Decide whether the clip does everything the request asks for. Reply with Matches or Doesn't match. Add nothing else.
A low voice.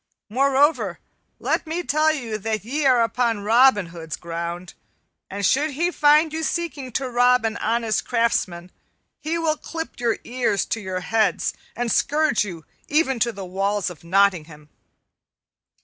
Doesn't match